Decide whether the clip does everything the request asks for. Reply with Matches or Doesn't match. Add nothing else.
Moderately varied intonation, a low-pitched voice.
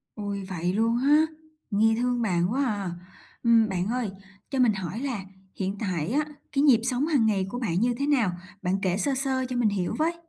Doesn't match